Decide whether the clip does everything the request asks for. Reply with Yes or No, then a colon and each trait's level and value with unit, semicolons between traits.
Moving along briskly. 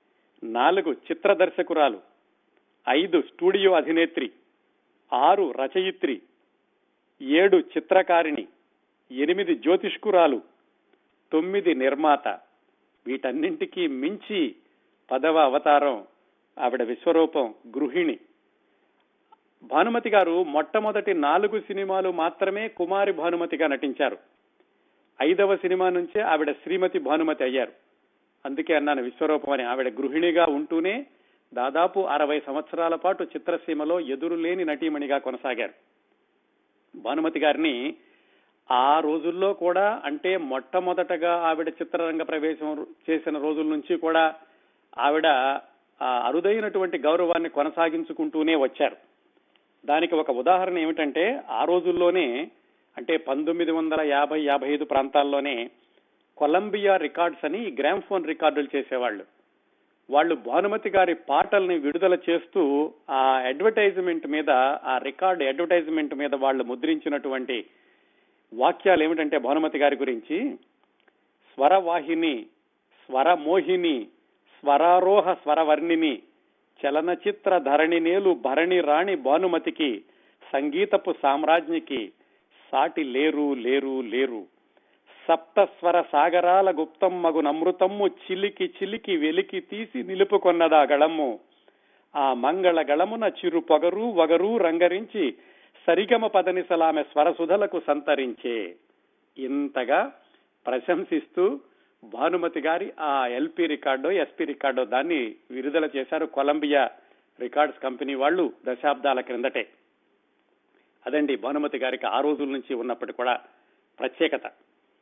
No: average, 95 wpm